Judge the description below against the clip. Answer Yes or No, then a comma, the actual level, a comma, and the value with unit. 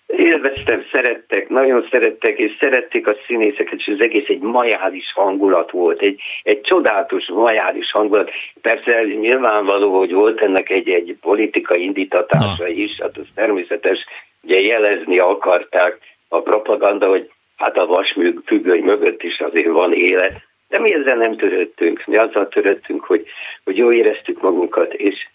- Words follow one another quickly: No, average, 145 wpm